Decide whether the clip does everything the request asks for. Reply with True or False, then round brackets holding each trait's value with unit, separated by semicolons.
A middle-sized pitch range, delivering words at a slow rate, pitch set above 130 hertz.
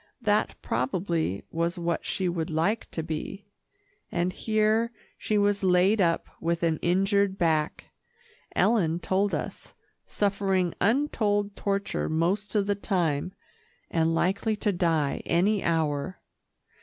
True (3.6 semitones; 125 wpm; 185 Hz)